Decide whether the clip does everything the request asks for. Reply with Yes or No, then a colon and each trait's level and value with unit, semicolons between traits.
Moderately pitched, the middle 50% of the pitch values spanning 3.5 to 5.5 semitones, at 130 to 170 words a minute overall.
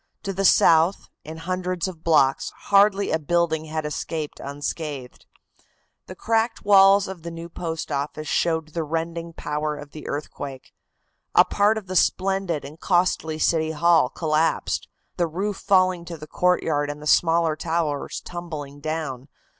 No: medium, 165 Hz; average, 3.0 semitones; average, 155 wpm